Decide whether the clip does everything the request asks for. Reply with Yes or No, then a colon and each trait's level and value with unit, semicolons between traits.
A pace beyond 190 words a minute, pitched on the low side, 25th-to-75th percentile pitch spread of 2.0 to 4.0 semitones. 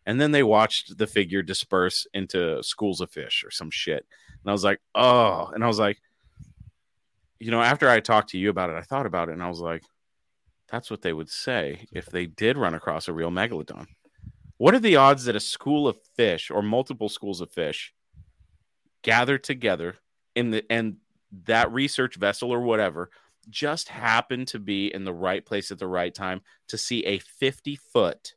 No: average, 200 wpm; low, 110 Hz; average, 5.2 semitones